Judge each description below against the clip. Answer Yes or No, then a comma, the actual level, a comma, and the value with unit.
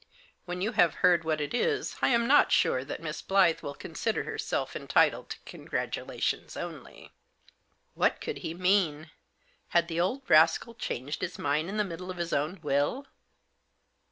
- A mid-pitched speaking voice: Yes, medium, 175 Hz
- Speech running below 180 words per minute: Yes, average, 170 wpm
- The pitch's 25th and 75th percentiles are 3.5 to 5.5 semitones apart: Yes, average, 4.3 semitones